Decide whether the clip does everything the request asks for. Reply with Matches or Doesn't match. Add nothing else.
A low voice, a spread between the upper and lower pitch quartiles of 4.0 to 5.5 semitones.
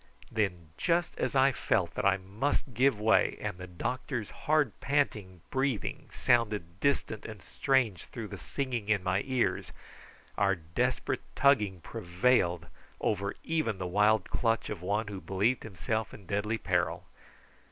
Matches